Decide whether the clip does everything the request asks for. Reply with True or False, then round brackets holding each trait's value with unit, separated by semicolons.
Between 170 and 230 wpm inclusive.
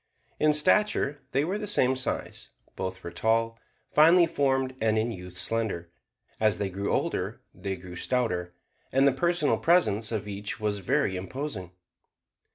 False (155 wpm)